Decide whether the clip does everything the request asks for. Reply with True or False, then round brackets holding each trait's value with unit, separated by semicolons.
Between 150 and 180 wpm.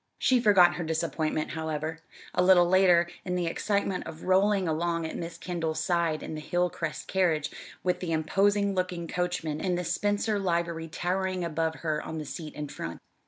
True (175 wpm)